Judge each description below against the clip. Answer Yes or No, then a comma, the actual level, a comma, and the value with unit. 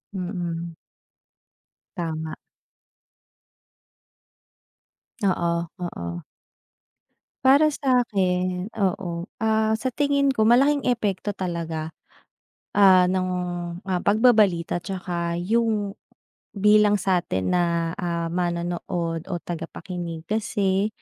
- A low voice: No, medium, 185 Hz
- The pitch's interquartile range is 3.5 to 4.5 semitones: Yes, average, 3.8 semitones